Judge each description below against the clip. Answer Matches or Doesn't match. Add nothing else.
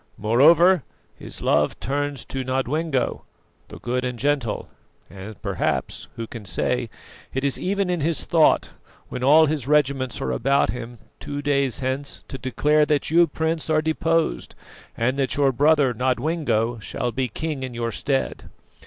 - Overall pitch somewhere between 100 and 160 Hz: Matches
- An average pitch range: Matches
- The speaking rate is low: Doesn't match